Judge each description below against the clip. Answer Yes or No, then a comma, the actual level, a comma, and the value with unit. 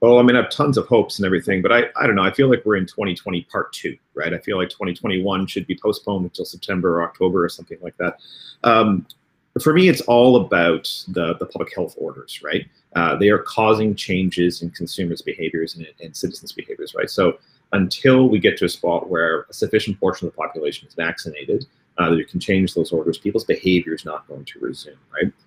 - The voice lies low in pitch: Yes, low, 100 Hz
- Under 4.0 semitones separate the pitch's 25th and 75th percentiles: No, wide, 5.6 semitones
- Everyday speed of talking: No, fast, 225 wpm